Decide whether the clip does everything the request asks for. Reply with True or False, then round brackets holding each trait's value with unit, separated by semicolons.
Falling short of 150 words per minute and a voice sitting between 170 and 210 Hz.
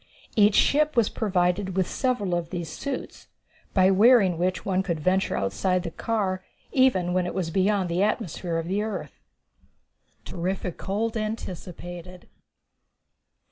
True (140 wpm; 185 Hz)